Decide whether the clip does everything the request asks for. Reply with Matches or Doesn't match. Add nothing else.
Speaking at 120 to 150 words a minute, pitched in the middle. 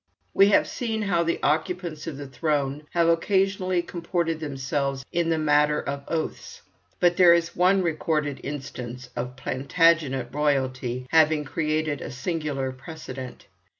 Matches